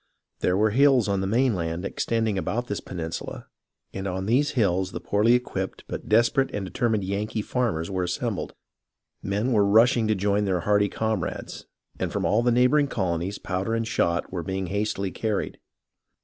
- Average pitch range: Yes, average, 3.3 semitones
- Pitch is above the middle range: No, low, 105 Hz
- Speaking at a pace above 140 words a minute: Yes, average, 170 wpm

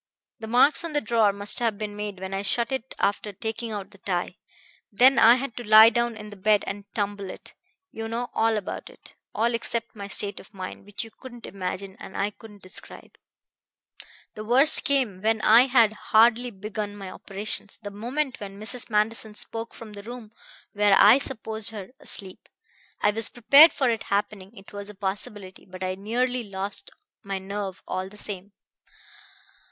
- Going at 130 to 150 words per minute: No, average, 185 wpm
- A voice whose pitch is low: No, high, 210 Hz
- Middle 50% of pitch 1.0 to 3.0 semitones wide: Yes, narrow, 2.6 semitones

